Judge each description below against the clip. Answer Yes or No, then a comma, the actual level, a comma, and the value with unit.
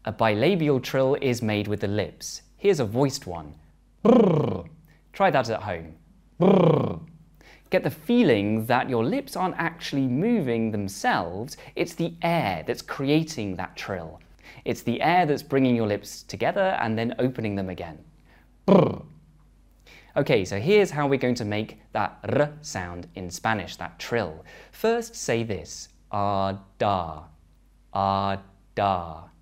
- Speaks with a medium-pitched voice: No, low, 110 Hz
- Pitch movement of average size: No, wide, 8.0 semitones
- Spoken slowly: No, average, 145 wpm